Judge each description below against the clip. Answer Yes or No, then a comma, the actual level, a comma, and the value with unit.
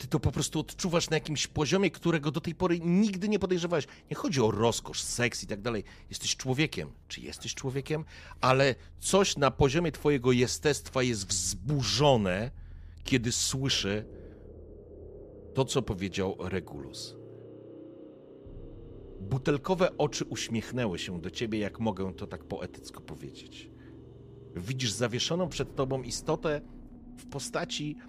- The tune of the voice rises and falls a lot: Yes, wide, 7.0 semitones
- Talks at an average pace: Yes, average, 130 wpm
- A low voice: Yes, low, 125 Hz